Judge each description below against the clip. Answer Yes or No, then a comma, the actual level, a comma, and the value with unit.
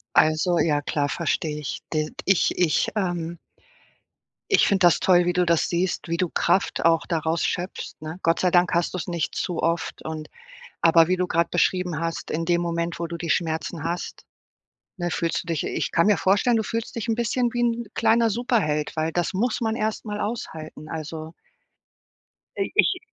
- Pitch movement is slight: No, average, 3.2 semitones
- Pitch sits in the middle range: Yes, medium, 175 Hz